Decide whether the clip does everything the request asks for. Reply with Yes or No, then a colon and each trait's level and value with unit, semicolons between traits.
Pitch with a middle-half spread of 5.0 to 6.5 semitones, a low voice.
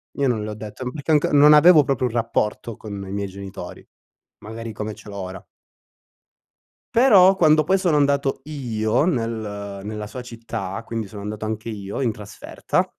Yes: average, 5.3 semitones; low, 115 Hz